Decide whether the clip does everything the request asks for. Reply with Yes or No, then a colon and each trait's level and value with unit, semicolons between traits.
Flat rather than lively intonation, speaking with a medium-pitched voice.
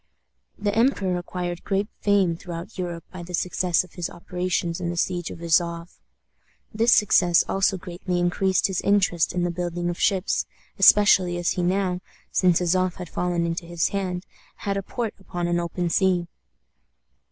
Yes: narrow, 1.8 semitones; medium, 180 Hz